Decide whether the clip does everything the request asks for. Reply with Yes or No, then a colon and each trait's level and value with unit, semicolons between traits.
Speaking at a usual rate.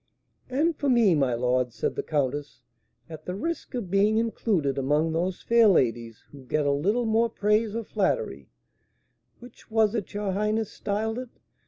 Yes: average, 170 wpm